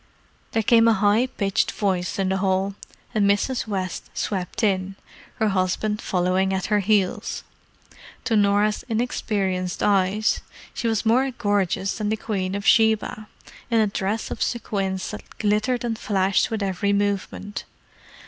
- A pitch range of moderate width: No, narrow, 2.3 semitones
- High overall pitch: Yes, high, 205 Hz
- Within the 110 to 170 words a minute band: Yes, average, 150 wpm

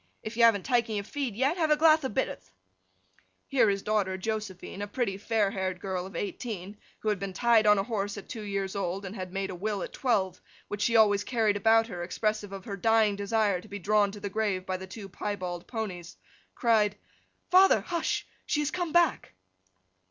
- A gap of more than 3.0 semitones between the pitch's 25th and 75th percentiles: No, average, 2.7 semitones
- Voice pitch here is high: Yes, high, 205 Hz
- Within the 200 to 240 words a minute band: Yes, fast, 205 wpm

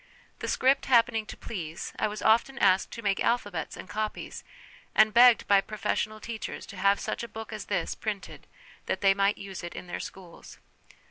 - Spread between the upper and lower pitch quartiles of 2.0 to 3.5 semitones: Yes, narrow, 2.4 semitones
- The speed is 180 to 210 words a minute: Yes, average, 195 wpm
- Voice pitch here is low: No, high, 210 Hz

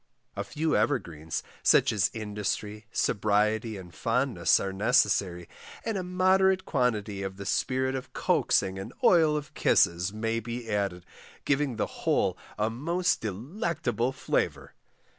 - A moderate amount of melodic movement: No, wide, 6.3 semitones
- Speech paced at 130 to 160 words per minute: Yes, slow, 135 wpm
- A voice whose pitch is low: Yes, low, 115 Hz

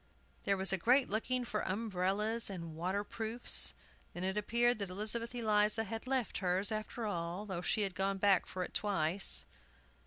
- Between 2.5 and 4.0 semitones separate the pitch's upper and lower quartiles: Yes, average, 3.0 semitones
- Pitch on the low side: No, high, 205 Hz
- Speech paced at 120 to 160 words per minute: No, average, 175 wpm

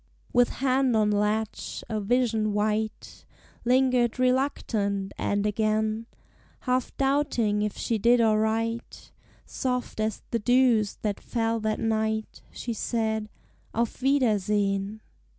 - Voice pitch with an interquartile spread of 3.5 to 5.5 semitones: No, narrow, 2.5 semitones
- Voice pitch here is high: Yes, high, 220 Hz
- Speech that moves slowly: Yes, slow, 115 wpm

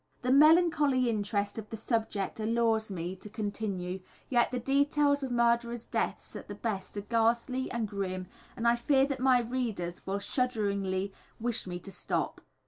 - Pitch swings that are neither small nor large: Yes, average, 4.0 semitones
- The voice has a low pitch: No, high, 230 Hz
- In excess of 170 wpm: No, average, 165 wpm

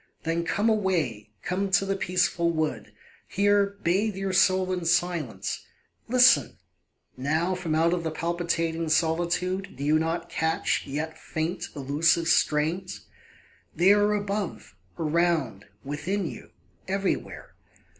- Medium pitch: Yes, medium, 170 Hz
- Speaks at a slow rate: Yes, slow, 120 wpm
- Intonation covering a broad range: No, average, 3.1 semitones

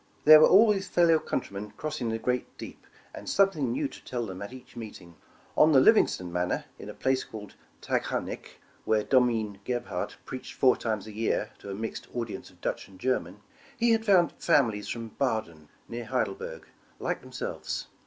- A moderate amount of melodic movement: No, wide, 6.5 semitones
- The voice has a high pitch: No, low, 120 Hz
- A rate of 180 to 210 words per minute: Yes, average, 190 wpm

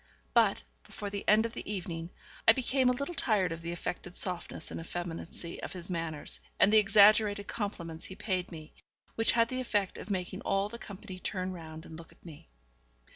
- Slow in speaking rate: No, average, 195 wpm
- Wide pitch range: No, average, 4.0 semitones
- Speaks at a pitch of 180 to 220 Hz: Yes, high, 190 Hz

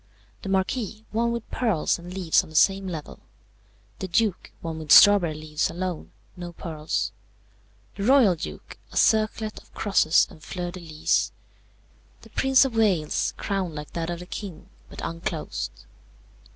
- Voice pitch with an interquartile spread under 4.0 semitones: No, average, 4.6 semitones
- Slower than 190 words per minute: Yes, average, 155 wpm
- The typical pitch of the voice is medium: Yes, medium, 180 Hz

